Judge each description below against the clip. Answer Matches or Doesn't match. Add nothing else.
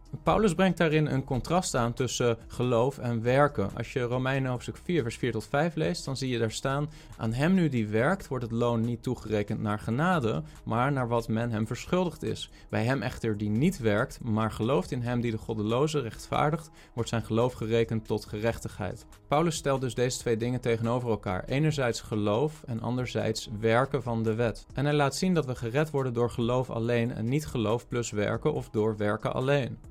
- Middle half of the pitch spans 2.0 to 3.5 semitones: Doesn't match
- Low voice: Matches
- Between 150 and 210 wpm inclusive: Matches